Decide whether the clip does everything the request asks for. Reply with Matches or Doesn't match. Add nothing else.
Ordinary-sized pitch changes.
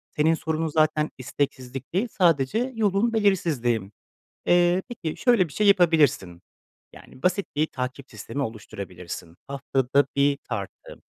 Doesn't match